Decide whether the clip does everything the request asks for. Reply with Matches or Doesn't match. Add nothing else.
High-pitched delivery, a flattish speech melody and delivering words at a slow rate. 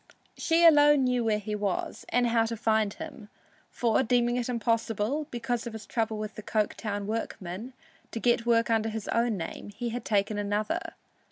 Doesn't match